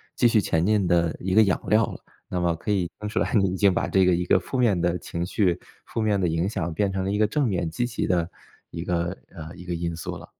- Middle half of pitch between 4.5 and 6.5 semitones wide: No, average, 3.4 semitones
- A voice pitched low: Yes, very low, 90 Hz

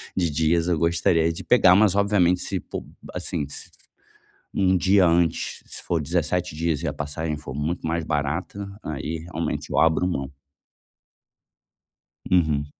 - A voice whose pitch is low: Yes, very low, 85 Hz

